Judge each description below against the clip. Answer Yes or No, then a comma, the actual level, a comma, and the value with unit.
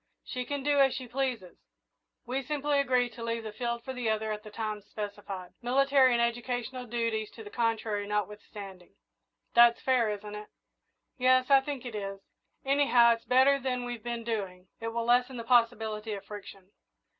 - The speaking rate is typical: Yes, average, 180 wpm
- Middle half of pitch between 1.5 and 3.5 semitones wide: Yes, average, 3.2 semitones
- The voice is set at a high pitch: Yes, high, 235 Hz